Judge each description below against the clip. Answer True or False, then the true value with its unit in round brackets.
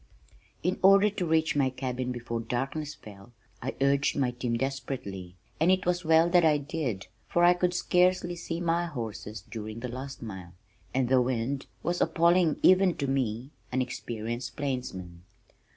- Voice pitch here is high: False (135 Hz)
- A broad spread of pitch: True (5.9 semitones)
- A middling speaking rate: True (165 wpm)